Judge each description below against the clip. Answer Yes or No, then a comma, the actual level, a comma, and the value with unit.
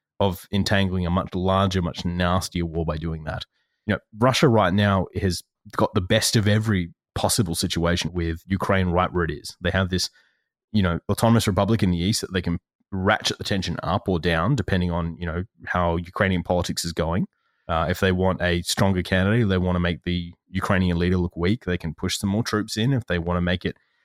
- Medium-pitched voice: No, very low, 95 Hz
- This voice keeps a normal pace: No, fast, 215 wpm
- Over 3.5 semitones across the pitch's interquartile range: No, average, 2.7 semitones